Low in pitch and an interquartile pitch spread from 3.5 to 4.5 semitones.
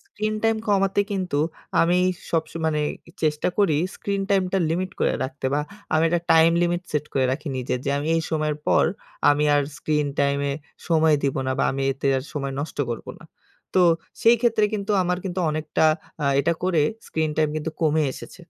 No: medium, 160 Hz; average, 3.8 semitones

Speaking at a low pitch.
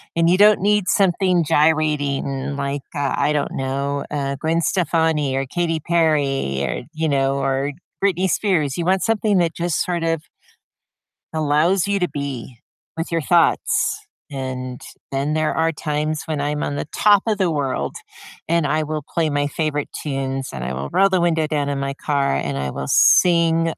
No: medium, 150 Hz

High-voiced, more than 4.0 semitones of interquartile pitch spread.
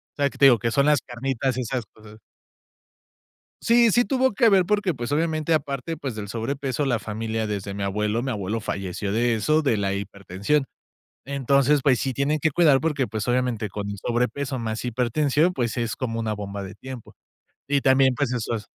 No: low, 125 Hz; average, 4.6 semitones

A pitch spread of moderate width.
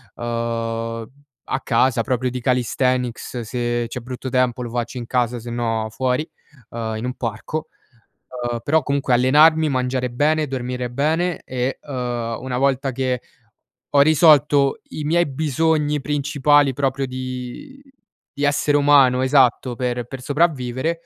Yes: average, 3.1 semitones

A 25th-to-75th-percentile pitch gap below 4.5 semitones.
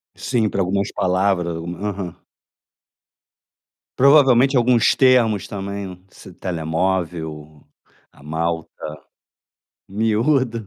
No: average, 5.1 semitones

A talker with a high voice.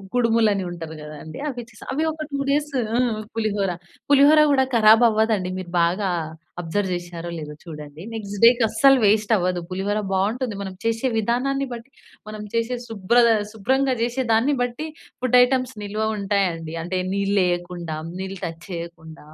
Yes: high, 210 Hz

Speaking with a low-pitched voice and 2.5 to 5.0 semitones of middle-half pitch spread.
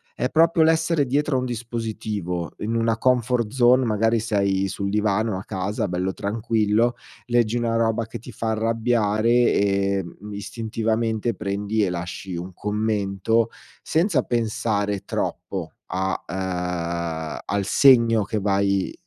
Yes: low, 110 Hz; average, 2.9 semitones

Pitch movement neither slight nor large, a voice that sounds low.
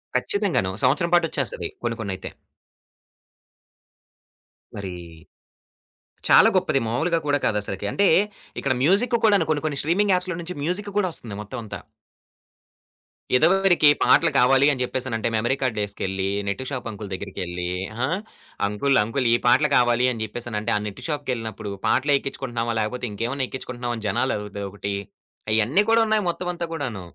No: wide, 6.7 semitones; low, 125 Hz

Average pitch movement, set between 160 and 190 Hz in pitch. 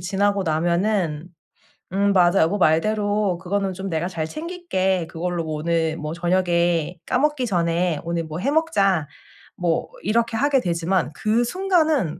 Yes: average, 4.1 semitones; medium, 185 Hz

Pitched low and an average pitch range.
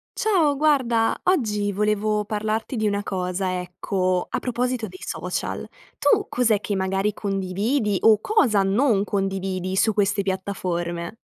No: high, 205 Hz; average, 3.0 semitones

